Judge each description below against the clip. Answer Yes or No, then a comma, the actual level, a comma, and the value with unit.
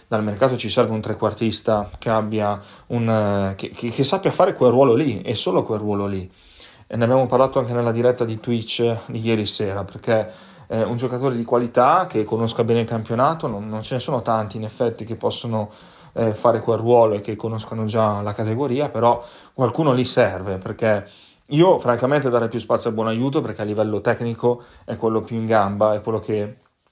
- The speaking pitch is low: Yes, low, 115 Hz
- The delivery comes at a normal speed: No, fast, 205 wpm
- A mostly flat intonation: Yes, narrow, 1.9 semitones